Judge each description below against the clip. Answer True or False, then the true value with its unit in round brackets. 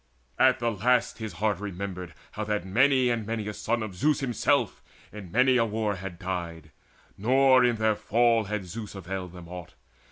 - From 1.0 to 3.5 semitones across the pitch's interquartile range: False (4.0 semitones)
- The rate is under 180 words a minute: False (185 wpm)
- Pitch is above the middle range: False (105 Hz)